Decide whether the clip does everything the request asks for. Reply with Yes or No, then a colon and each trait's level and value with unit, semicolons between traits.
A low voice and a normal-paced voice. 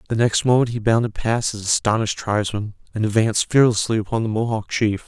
Yes: low, 110 Hz; average, 190 wpm